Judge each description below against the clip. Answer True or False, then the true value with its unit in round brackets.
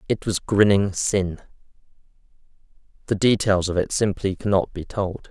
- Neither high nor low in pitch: False (100 Hz)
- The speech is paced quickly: False (135 wpm)